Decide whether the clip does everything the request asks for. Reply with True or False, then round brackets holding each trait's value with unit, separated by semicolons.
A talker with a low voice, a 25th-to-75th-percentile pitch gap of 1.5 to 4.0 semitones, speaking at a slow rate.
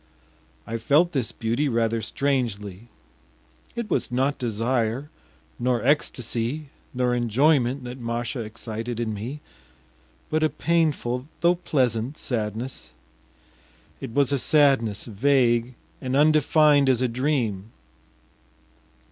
True (125 Hz; 3.7 semitones; 110 wpm)